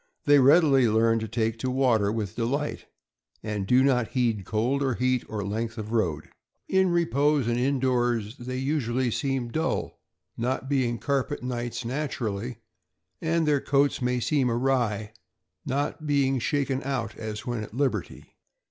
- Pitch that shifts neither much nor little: Yes, average, 3.4 semitones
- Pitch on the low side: Yes, low, 125 Hz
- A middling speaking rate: Yes, average, 155 wpm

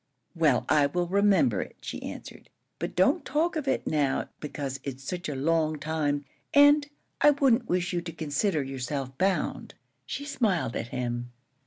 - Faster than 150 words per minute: Yes, average, 165 wpm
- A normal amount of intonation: No, wide, 6.5 semitones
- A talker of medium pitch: Yes, medium, 160 Hz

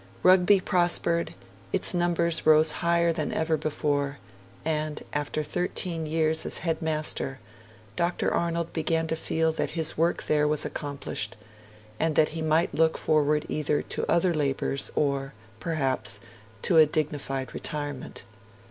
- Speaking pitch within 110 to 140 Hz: No, medium, 155 Hz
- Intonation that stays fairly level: Yes, narrow, 2.1 semitones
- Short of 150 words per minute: Yes, slow, 135 wpm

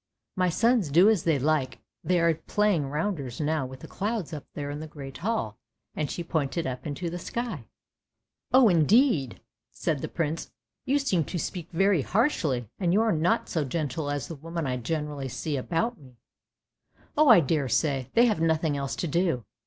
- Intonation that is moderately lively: Yes, average, 4.8 semitones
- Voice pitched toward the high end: No, medium, 160 Hz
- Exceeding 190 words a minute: Yes, average, 200 wpm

